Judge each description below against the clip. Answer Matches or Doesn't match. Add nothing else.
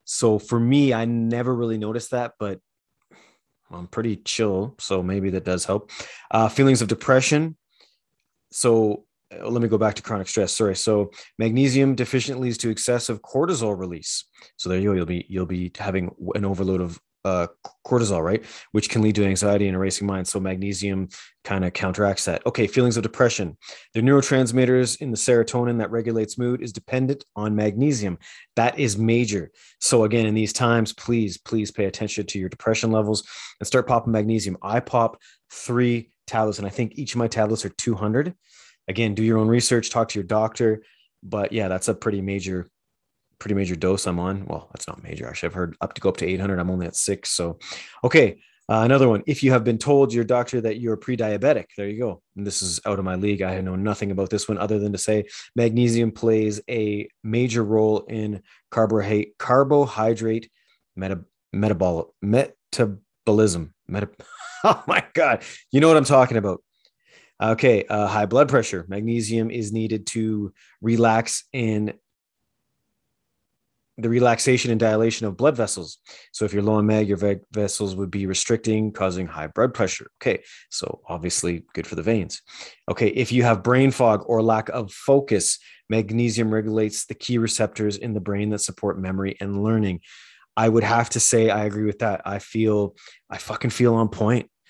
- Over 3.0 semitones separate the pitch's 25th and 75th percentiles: Doesn't match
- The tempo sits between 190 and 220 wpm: Doesn't match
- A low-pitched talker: Matches